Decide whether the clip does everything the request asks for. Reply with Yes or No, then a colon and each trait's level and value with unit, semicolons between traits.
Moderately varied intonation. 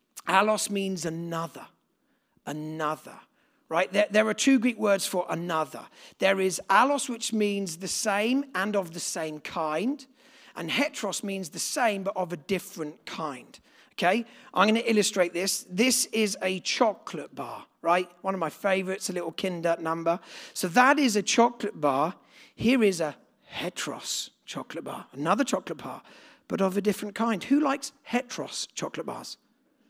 Yes: average, 4.7 semitones